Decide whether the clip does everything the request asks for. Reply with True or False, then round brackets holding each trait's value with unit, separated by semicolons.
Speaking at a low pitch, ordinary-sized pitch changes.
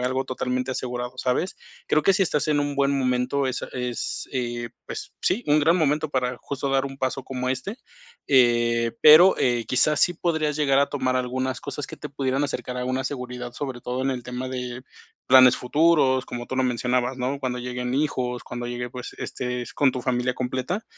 False (130 Hz; 2.2 semitones)